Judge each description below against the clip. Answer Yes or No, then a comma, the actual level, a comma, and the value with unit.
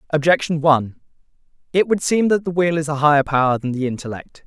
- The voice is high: No, medium, 155 Hz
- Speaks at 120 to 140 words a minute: No, average, 200 wpm